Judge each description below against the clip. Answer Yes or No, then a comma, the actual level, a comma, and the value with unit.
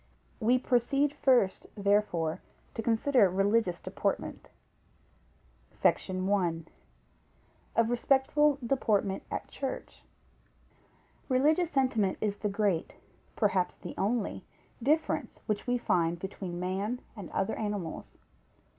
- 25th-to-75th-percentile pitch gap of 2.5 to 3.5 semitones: No, average, 4.8 semitones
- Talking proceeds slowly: Yes, slow, 100 wpm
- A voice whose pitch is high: Yes, high, 210 Hz